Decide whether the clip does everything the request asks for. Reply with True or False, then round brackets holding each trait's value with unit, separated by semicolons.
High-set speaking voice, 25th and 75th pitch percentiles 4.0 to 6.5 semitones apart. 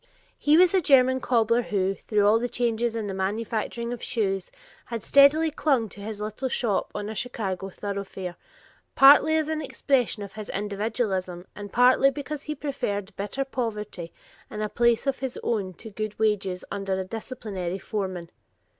True (220 Hz; 4.3 semitones)